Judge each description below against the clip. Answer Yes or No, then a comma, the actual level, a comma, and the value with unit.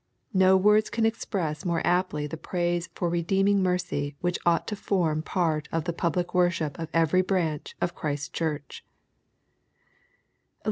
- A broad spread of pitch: No, average, 3.0 semitones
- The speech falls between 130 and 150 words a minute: Yes, average, 145 wpm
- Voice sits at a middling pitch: Yes, medium, 175 Hz